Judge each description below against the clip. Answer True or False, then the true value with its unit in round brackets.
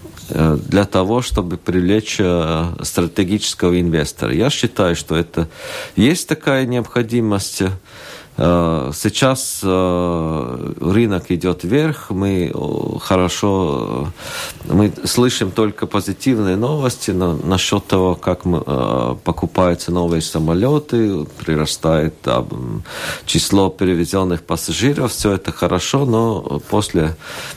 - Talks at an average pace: False (85 wpm)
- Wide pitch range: False (3.9 semitones)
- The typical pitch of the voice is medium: False (95 Hz)